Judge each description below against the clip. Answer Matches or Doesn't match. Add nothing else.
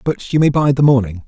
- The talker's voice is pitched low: Matches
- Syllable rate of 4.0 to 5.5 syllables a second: Doesn't match